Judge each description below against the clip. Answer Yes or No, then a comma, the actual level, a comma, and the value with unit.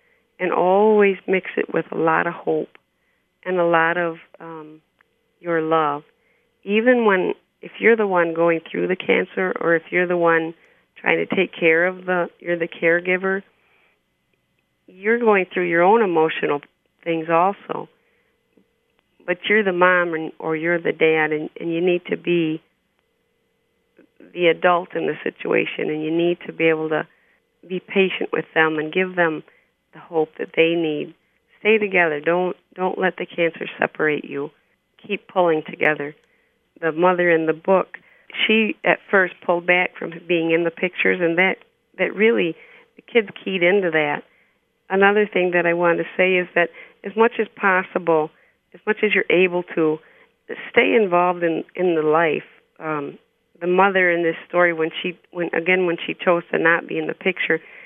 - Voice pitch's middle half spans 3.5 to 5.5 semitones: No, narrow, 2.4 semitones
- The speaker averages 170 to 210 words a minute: Yes, average, 175 wpm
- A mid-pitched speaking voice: Yes, medium, 175 Hz